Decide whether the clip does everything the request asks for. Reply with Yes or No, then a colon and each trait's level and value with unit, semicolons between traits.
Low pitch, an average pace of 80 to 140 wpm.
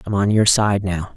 No: low, 100 Hz; fast, 260 wpm